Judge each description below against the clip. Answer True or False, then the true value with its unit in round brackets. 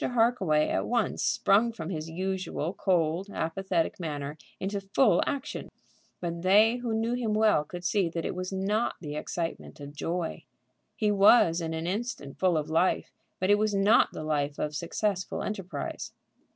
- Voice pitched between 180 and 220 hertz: True (185 Hz)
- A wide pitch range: False (4.4 semitones)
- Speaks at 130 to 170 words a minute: True (165 wpm)